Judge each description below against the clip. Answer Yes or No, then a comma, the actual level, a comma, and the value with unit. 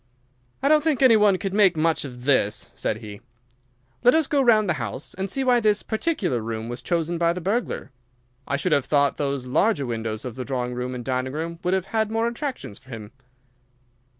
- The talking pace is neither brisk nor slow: No, fast, 210 wpm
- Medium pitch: Yes, medium, 160 Hz